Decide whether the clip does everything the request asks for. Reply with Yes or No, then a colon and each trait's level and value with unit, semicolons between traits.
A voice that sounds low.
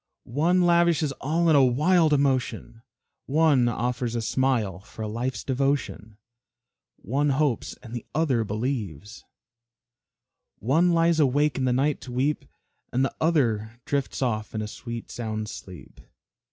Yes: low, 130 Hz